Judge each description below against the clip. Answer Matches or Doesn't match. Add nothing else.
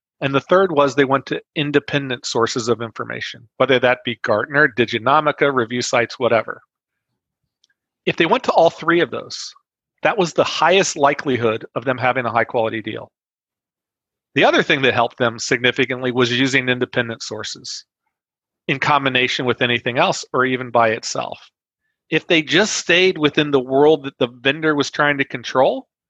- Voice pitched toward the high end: Doesn't match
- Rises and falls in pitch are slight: Doesn't match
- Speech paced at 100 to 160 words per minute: Doesn't match